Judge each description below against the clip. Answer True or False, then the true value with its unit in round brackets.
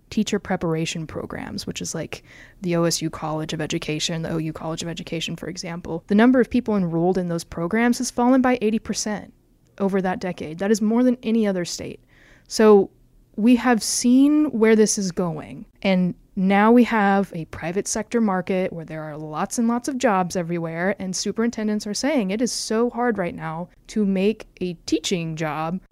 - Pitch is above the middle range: True (195 Hz)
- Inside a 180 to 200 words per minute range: True (185 wpm)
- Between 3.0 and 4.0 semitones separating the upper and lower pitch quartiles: False (5.0 semitones)